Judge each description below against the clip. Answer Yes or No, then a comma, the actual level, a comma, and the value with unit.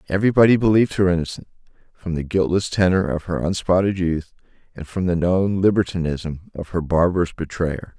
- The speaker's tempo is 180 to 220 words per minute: No, average, 165 wpm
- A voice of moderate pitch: No, very low, 90 Hz